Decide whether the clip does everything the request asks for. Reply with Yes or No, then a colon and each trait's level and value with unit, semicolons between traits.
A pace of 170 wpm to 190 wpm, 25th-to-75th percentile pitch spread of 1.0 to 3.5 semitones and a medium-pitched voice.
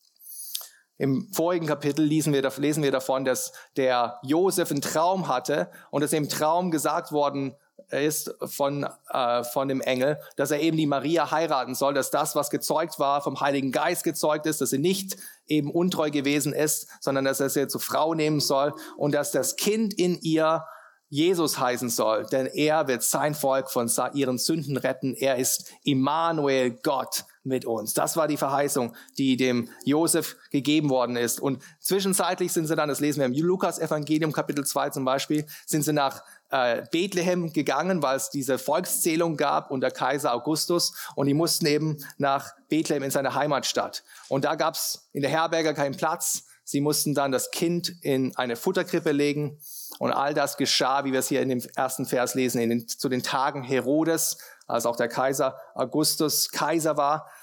Yes: average, 180 wpm; average, 2.8 semitones; medium, 145 Hz